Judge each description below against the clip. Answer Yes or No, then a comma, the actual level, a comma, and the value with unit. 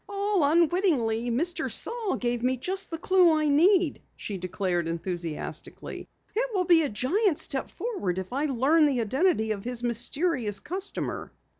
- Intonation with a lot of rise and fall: Yes, wide, 8.2 semitones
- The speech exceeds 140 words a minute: Yes, average, 155 wpm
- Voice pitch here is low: No, very high, 290 Hz